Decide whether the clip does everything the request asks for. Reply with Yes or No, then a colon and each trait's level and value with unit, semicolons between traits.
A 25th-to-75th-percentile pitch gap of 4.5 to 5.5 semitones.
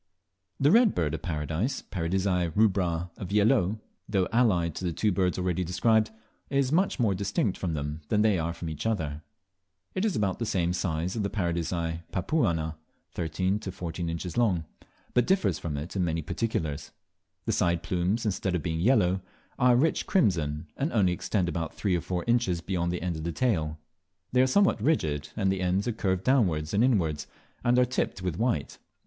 Yes: average, 4.9 semitones